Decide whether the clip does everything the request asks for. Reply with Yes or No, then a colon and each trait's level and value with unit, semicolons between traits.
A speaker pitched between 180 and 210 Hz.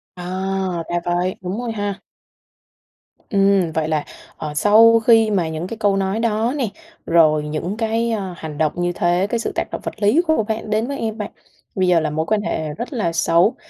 Yes: high, 195 Hz